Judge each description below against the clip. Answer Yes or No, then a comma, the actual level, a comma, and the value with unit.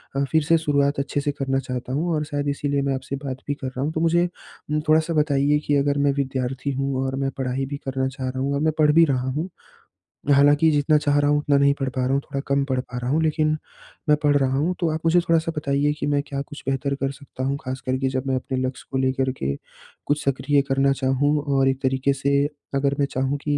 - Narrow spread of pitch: Yes, narrow, 1.7 semitones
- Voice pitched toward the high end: No, medium, 140 Hz